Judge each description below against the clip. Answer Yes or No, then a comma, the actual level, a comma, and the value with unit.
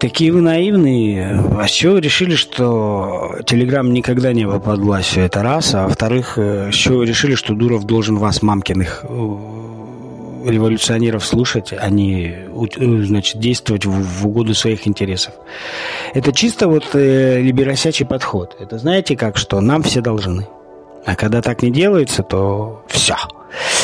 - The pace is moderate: Yes, average, 135 wpm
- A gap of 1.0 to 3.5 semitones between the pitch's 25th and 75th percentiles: No, average, 4.3 semitones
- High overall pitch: No, low, 115 Hz